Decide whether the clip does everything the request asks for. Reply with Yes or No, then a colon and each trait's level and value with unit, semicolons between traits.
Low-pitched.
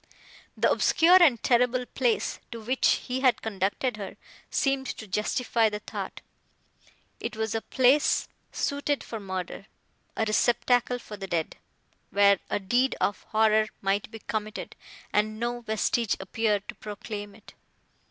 No: high, 220 Hz